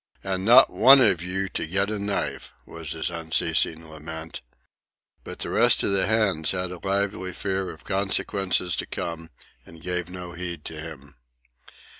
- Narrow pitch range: No, average, 3.0 semitones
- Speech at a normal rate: Yes, average, 165 wpm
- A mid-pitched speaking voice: No, very low, 90 Hz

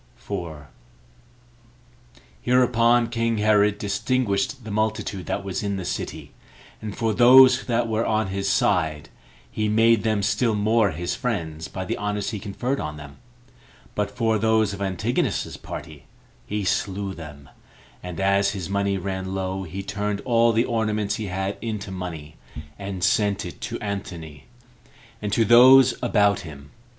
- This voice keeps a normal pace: Yes, average, 150 wpm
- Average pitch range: Yes, average, 3.0 semitones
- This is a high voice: No, low, 100 Hz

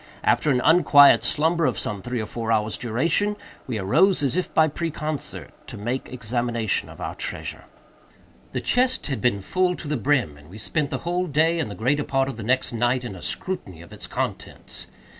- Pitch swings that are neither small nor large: No, wide, 6.2 semitones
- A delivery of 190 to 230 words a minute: Yes, average, 200 wpm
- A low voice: Yes, low, 130 Hz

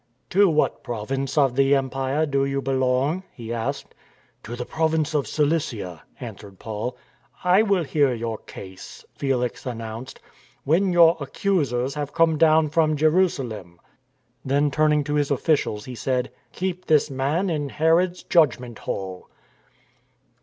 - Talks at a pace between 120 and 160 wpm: Yes, average, 155 wpm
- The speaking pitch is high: No, medium, 140 Hz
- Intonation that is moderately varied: Yes, average, 4.4 semitones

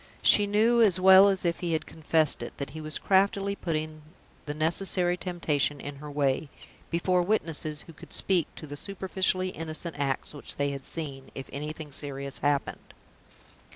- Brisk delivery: No, average, 170 wpm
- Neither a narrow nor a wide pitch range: Yes, average, 4.2 semitones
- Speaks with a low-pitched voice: No, medium, 160 Hz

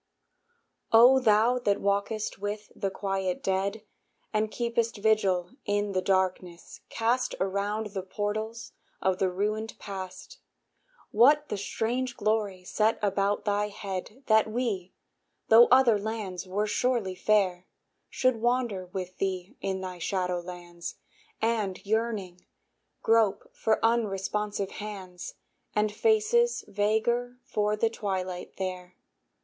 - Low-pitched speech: No, high, 205 Hz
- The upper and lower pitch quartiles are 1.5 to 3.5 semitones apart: Yes, average, 3.0 semitones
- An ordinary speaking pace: No, slow, 120 wpm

